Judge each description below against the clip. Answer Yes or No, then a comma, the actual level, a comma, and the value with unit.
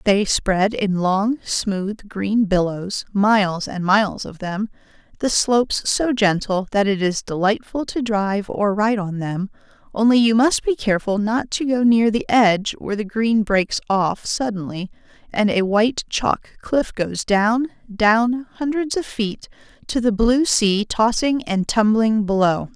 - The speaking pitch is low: No, high, 215 Hz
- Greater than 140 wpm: Yes, average, 165 wpm